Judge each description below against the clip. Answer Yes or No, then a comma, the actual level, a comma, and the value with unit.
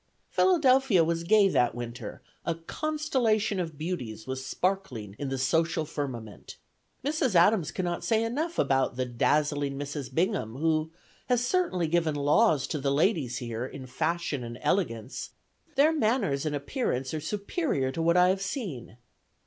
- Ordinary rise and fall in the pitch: No, wide, 7.5 semitones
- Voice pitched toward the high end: No, medium, 160 Hz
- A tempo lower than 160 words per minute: Yes, average, 150 wpm